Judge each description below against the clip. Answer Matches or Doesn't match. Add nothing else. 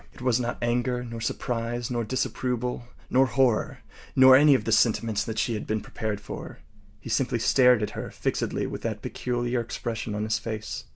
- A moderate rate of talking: Matches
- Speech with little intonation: Matches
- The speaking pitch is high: Doesn't match